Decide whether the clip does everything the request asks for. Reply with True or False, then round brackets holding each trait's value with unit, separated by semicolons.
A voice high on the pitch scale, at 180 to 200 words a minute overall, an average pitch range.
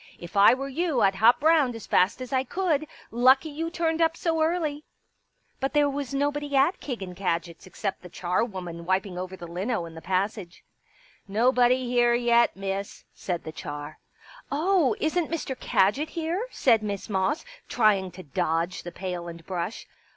False (235 Hz; 190 wpm; 7.8 semitones)